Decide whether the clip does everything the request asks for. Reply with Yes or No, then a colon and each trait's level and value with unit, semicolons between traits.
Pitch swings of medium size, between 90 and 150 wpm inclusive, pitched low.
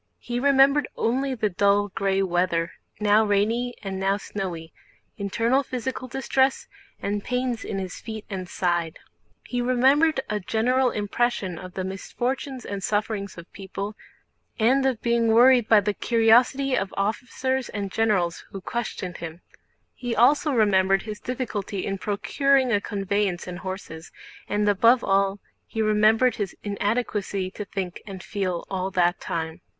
No: average, 4.0 semitones; average, 145 wpm; high, 210 Hz